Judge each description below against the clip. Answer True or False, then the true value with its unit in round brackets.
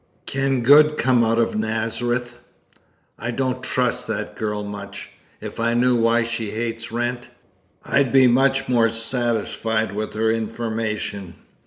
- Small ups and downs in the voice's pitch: True (2.0 semitones)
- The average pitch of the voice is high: False (115 Hz)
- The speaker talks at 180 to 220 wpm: False (140 wpm)